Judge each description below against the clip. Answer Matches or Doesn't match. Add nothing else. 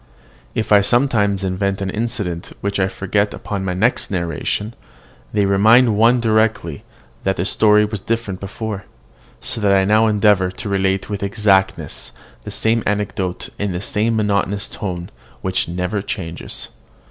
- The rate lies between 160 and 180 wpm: Doesn't match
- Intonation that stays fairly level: Matches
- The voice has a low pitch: Matches